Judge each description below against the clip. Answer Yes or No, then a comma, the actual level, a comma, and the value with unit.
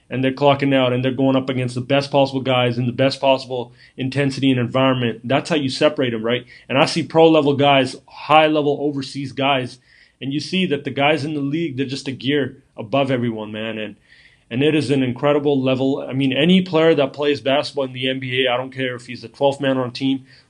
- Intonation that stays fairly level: Yes, narrow, 1.8 semitones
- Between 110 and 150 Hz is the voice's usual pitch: Yes, low, 135 Hz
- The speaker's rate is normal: No, fast, 235 wpm